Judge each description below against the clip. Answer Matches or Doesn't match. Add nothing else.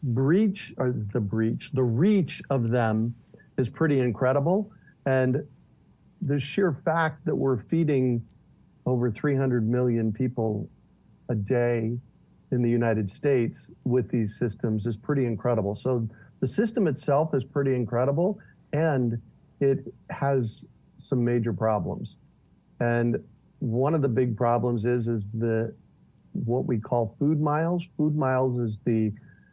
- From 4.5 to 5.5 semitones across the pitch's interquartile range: Doesn't match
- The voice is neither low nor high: Doesn't match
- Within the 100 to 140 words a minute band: Matches